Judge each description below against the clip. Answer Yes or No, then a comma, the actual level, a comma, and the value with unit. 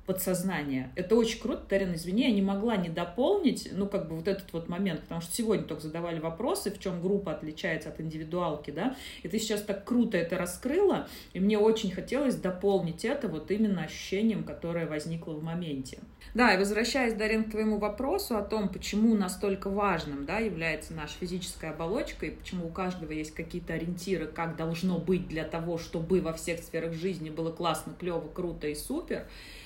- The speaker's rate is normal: No, fast, 185 wpm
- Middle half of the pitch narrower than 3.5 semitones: No, average, 3.9 semitones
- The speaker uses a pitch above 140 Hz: Yes, medium, 185 Hz